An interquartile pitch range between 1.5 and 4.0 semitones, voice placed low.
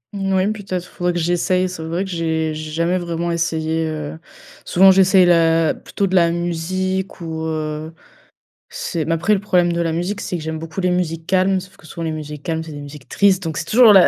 No: narrow, 2.6 semitones; medium, 170 Hz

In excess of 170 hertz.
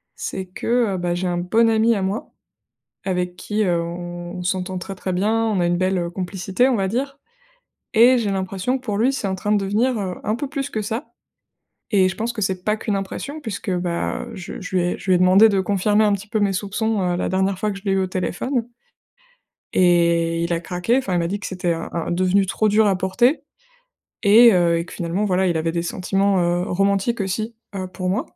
Yes: high, 190 Hz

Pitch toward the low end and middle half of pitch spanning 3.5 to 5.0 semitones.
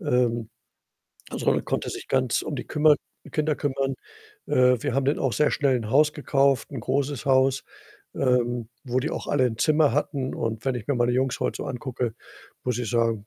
No: low, 130 Hz; average, 2.7 semitones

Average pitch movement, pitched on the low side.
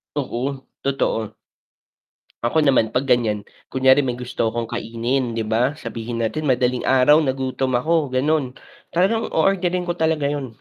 Yes: average, 3.7 semitones; low, 130 Hz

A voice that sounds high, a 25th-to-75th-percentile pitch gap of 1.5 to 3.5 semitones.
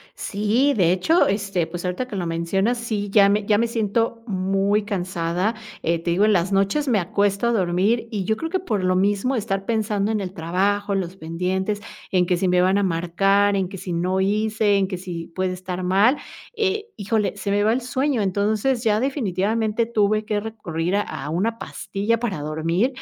Yes: high, 200 Hz; average, 3.1 semitones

